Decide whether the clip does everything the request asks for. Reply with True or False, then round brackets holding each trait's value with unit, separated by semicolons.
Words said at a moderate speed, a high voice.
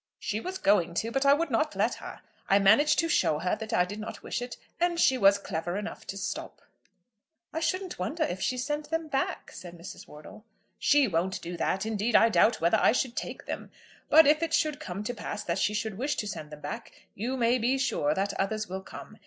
False (230 wpm; 220 Hz)